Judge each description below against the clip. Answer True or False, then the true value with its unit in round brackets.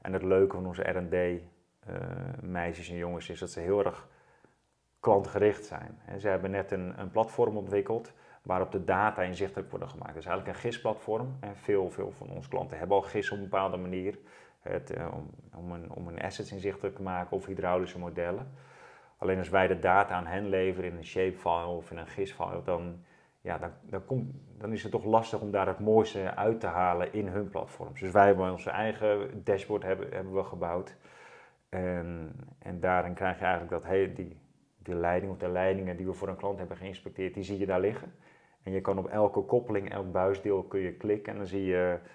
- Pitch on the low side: True (95 Hz)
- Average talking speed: False (210 wpm)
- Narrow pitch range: True (1.9 semitones)